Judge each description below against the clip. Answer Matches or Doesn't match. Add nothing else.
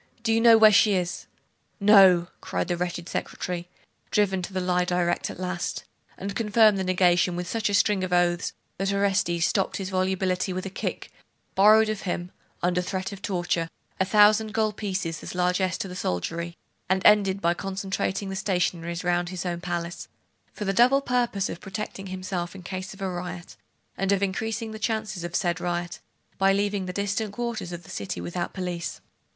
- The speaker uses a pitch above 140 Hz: Matches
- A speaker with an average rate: Matches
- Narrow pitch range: Matches